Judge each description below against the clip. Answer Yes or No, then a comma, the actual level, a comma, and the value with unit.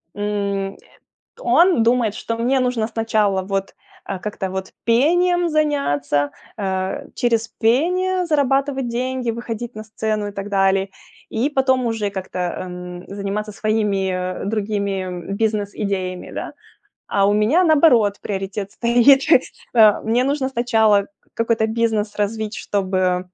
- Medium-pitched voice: No, high, 215 Hz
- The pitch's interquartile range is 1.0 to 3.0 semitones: No, average, 3.7 semitones